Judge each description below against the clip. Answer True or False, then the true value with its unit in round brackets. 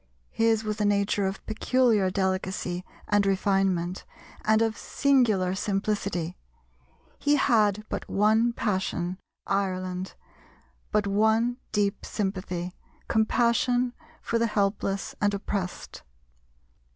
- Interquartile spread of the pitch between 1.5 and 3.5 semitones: True (2.6 semitones)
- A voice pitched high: True (205 Hz)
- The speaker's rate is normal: False (105 wpm)